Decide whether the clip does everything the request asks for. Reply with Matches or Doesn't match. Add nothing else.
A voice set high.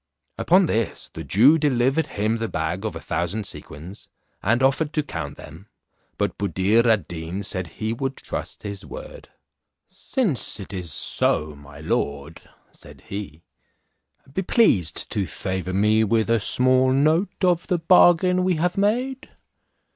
Doesn't match